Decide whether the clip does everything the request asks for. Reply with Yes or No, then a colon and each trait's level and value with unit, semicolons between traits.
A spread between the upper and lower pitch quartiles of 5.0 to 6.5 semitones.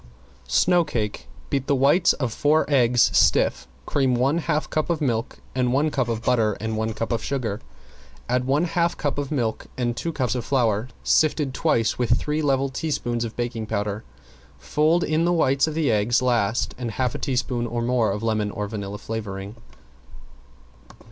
No: average, 4.3 semitones